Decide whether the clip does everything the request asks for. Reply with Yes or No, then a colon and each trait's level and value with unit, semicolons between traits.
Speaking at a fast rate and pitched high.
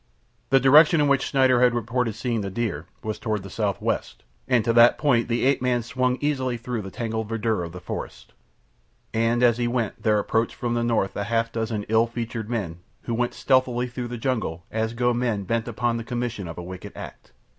No: fast, 215 wpm; low, 115 Hz